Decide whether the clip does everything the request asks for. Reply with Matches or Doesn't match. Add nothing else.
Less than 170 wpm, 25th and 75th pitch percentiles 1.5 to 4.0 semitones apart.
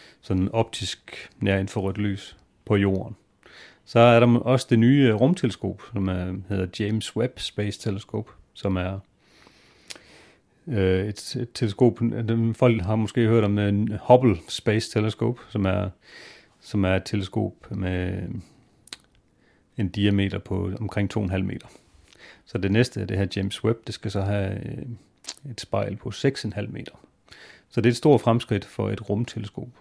Matches